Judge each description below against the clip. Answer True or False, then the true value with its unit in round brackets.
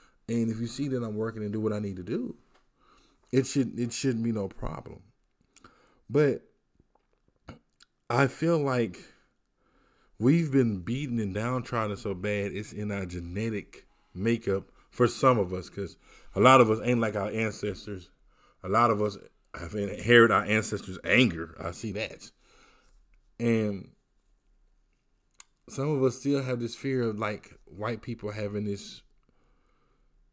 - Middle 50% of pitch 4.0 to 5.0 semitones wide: False (3.1 semitones)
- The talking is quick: False (150 wpm)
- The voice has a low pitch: True (110 Hz)